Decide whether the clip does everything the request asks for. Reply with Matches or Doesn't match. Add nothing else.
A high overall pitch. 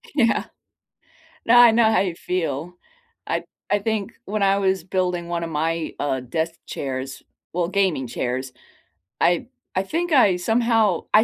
Doesn't match